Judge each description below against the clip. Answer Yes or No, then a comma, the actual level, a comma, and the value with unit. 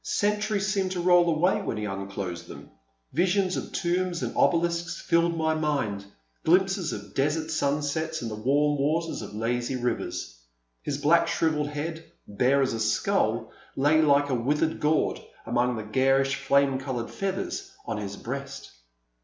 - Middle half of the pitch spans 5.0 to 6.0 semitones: Yes, wide, 5.4 semitones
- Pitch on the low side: No, medium, 145 Hz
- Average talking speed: Yes, average, 160 wpm